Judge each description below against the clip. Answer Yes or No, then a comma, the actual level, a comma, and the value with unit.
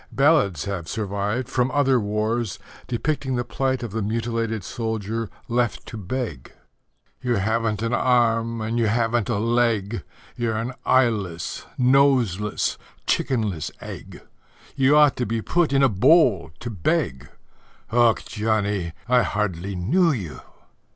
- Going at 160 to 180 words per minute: No, slow, 135 wpm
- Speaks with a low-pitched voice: Yes, low, 115 Hz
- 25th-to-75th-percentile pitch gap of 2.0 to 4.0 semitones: Yes, average, 3.3 semitones